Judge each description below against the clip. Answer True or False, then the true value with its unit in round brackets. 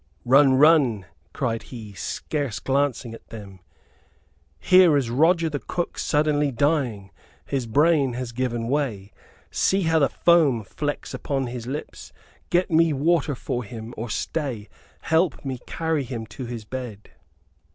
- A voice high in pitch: False (135 Hz)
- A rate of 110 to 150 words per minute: True (140 wpm)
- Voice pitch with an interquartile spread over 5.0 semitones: False (4.6 semitones)